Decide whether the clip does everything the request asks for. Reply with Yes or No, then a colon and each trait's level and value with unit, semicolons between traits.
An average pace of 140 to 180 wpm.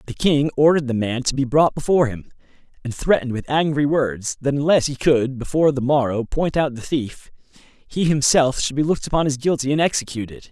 No: fast, 205 wpm